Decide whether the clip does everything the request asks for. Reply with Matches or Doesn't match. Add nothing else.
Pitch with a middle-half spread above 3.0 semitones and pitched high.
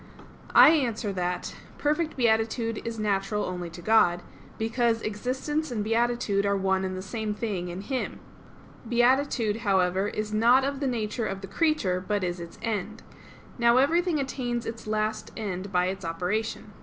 Matches